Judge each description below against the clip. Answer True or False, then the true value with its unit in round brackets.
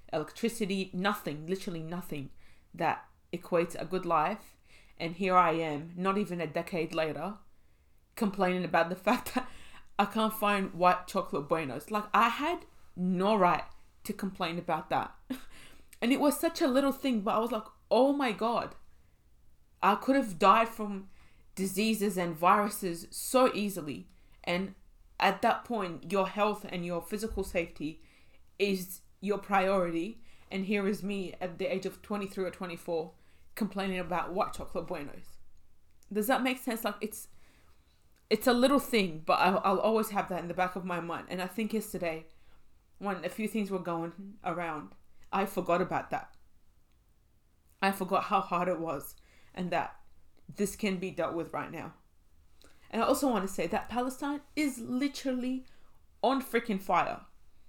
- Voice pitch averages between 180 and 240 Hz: True (190 Hz)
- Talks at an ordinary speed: True (165 wpm)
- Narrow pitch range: False (4.2 semitones)